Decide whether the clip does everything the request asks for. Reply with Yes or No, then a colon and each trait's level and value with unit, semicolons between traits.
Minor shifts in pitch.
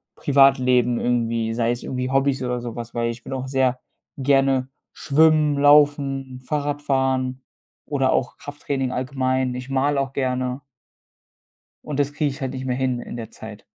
Yes: narrow, 1.8 semitones